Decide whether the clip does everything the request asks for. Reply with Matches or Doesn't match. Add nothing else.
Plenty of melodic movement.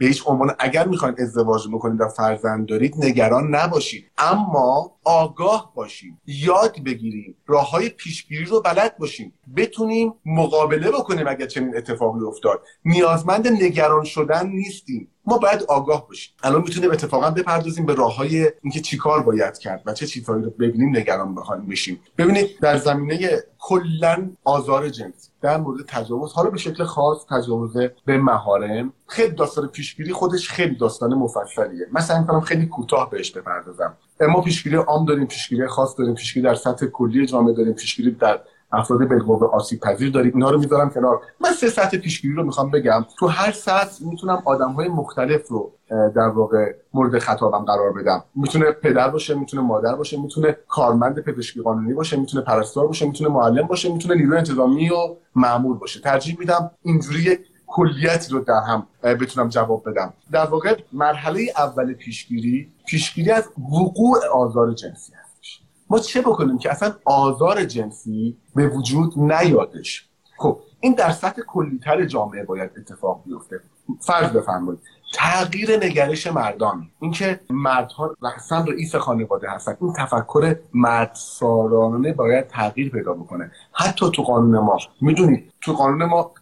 Matches